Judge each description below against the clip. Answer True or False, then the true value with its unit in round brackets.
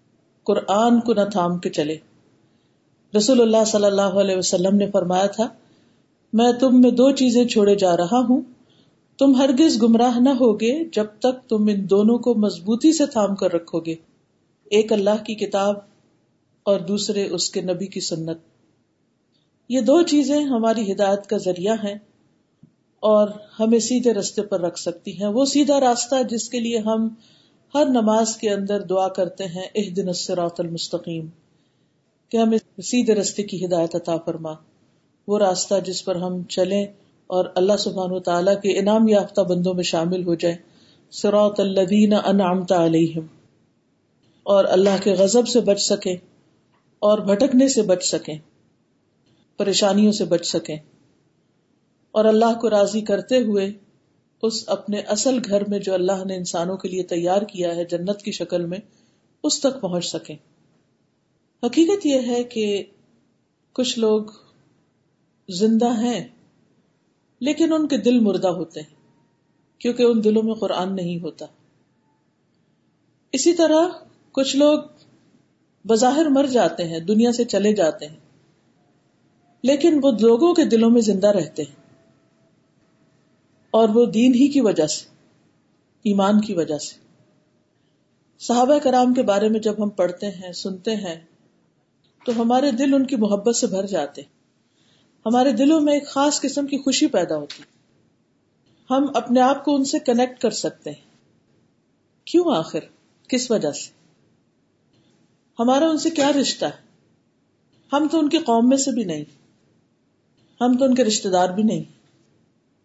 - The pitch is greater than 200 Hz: True (210 Hz)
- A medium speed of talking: True (150 wpm)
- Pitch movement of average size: True (4.8 semitones)